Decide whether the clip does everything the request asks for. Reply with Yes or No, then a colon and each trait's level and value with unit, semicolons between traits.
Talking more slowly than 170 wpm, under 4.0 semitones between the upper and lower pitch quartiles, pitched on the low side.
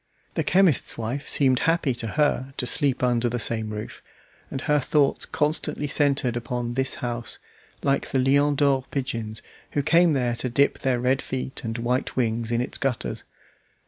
No: average, 175 wpm; average, 3.0 semitones; low, 130 Hz